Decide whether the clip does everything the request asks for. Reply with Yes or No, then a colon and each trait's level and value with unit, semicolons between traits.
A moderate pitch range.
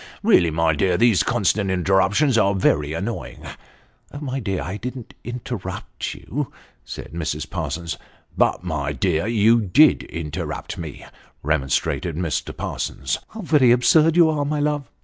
No: wide, 7.5 semitones